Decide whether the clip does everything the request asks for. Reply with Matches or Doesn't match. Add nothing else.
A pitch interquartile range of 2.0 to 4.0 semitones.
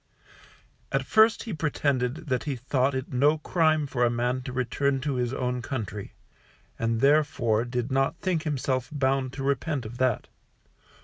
Matches